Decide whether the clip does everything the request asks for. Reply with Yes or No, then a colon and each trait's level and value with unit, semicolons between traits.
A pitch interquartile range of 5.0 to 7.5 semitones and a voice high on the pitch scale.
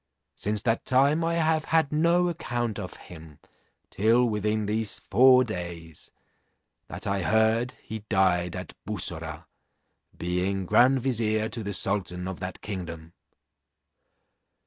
No: wide, 5.4 semitones; low, 105 Hz